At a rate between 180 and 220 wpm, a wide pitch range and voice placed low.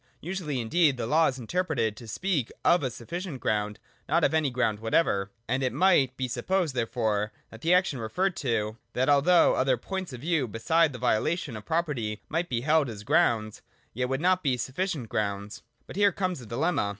Yes: average, 200 wpm; wide, 6.8 semitones; low, 130 Hz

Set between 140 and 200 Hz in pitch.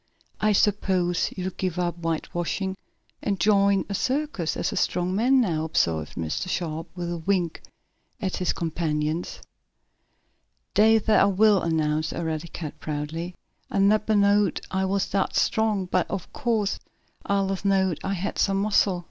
Yes: medium, 185 Hz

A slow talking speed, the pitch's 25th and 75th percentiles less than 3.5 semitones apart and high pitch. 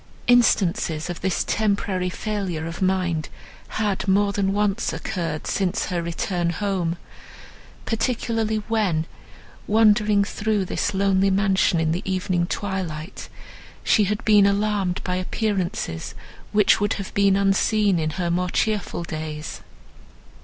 Yes: slow, 125 wpm; average, 3.0 semitones; high, 195 Hz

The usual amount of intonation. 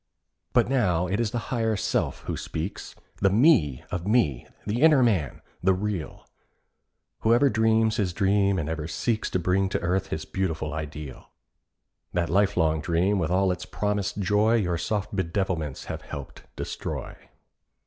Yes: average, 4.3 semitones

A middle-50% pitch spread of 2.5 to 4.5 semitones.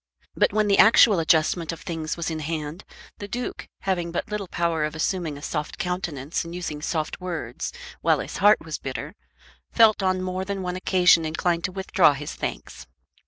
Yes: average, 3.2 semitones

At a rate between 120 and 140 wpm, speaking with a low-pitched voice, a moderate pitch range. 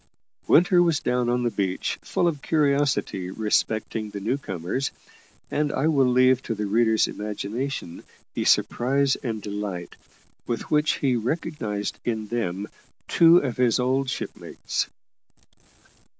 Yes: slow, 135 wpm; low, 120 Hz; average, 4.9 semitones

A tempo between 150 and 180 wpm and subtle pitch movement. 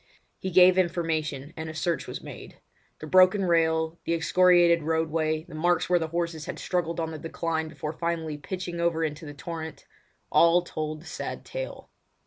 Yes: average, 165 wpm; narrow, 1.6 semitones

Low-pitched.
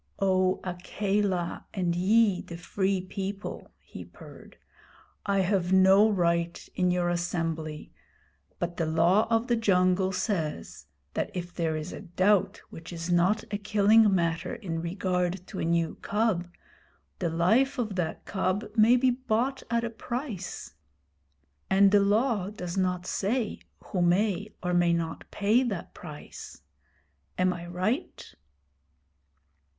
No: medium, 185 Hz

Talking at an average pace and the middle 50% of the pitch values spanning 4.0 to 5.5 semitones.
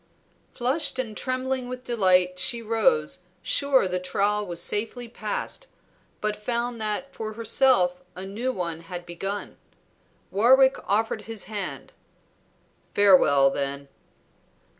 No: slow, 120 wpm; average, 5.1 semitones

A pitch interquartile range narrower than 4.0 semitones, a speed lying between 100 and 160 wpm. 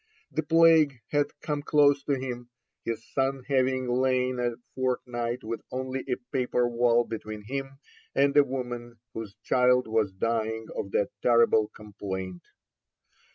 Yes: average, 2.8 semitones; average, 140 wpm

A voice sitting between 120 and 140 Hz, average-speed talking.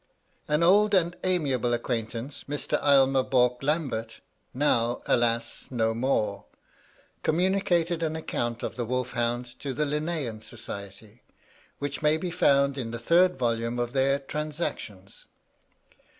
No: low, 135 Hz; slow, 130 wpm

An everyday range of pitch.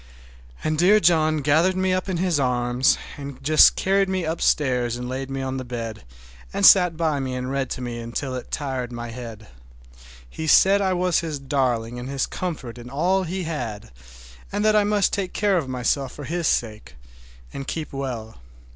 No: wide, 5.9 semitones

